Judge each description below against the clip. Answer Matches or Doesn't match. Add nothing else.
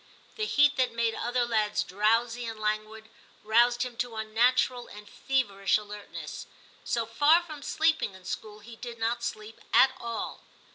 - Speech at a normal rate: Matches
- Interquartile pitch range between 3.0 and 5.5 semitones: Doesn't match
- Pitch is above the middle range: Matches